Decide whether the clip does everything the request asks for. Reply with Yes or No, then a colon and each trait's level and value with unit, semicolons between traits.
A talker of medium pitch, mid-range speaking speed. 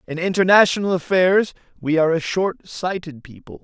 Yes: medium, 175 Hz; average, 150 wpm